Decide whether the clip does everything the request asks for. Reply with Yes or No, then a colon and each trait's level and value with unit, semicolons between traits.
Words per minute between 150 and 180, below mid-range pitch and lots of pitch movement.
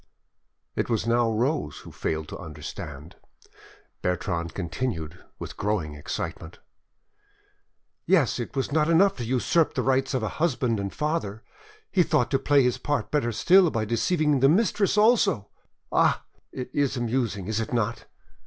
Yes: average, 155 wpm; low, 120 Hz; wide, 6.7 semitones